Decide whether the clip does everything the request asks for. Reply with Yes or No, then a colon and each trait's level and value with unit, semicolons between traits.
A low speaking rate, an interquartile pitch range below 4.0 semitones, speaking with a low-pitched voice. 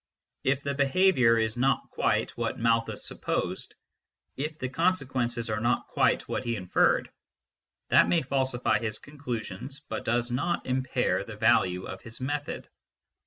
No: average, 145 wpm; average, 3.4 semitones; low, 125 Hz